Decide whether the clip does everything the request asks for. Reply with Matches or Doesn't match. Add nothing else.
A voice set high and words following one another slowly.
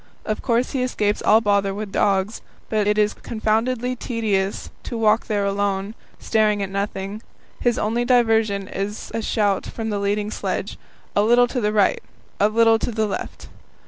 Doesn't match